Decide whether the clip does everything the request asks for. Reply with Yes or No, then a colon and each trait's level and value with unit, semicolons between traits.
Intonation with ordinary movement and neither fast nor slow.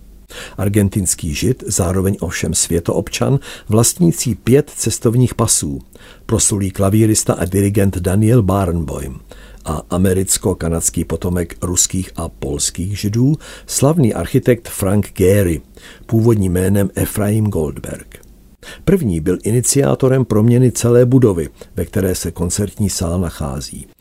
No: average, 4.6 semitones; slow, 105 wpm